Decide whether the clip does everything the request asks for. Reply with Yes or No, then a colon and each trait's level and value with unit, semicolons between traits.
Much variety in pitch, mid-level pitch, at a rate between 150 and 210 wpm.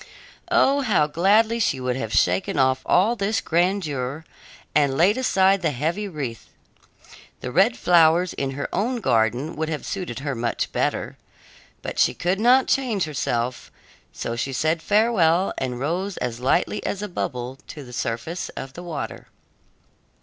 Yes: wide, 7.1 semitones; medium, 160 Hz; average, 155 wpm